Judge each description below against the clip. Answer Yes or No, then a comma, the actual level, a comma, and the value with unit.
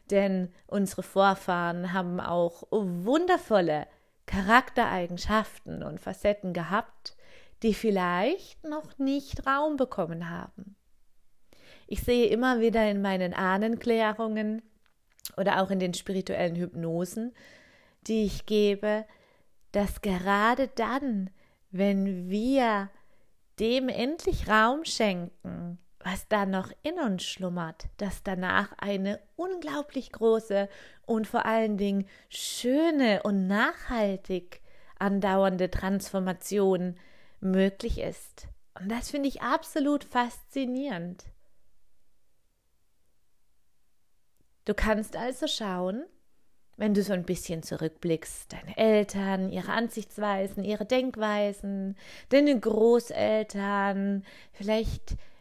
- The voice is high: Yes, high, 205 Hz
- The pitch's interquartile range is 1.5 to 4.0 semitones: Yes, average, 3.6 semitones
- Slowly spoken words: Yes, slow, 95 wpm